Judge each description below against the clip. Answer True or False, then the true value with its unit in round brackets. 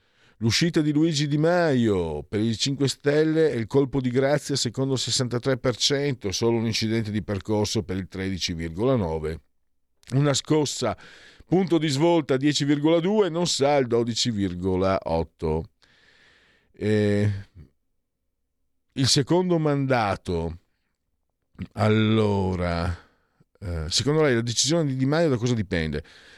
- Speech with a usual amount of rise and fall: False (7.3 semitones)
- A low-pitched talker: True (115 Hz)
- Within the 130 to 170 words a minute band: False (115 wpm)